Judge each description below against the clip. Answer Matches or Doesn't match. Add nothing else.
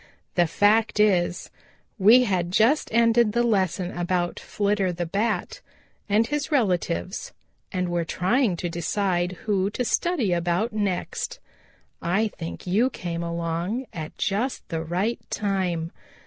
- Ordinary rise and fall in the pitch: Matches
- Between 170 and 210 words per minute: Doesn't match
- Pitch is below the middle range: Doesn't match